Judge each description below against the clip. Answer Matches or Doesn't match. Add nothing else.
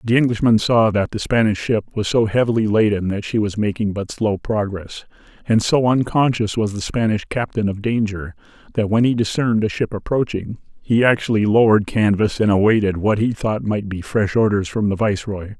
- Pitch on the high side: Doesn't match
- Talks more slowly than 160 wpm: Doesn't match